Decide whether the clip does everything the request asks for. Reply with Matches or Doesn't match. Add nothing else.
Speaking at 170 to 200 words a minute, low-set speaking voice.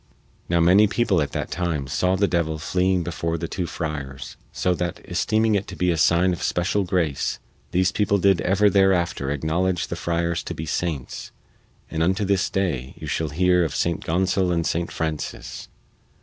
Matches